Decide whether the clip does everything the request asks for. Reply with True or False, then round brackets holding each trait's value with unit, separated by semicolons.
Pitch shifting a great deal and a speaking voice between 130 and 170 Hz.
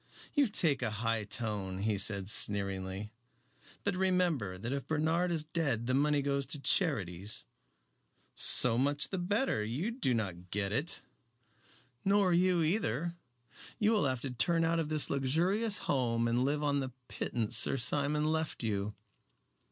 True (7.2 semitones; 140 Hz)